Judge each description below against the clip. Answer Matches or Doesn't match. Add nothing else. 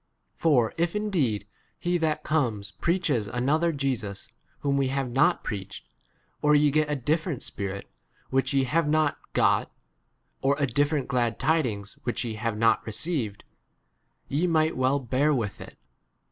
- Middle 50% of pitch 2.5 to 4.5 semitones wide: Doesn't match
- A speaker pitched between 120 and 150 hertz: Matches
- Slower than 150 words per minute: Doesn't match